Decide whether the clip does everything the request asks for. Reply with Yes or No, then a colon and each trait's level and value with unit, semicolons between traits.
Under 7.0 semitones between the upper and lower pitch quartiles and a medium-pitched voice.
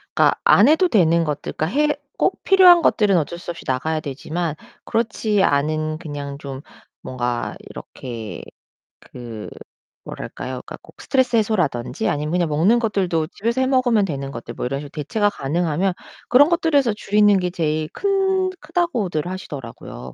No: wide, 8.1 semitones; medium, 175 Hz